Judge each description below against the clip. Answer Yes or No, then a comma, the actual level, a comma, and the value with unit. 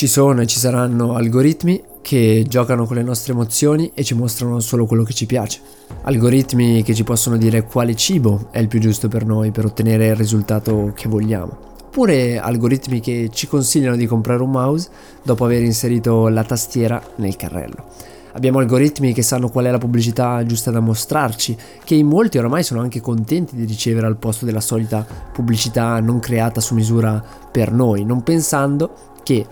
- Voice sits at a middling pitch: No, low, 120 Hz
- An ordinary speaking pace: No, fast, 180 wpm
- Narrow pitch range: Yes, narrow, 2.1 semitones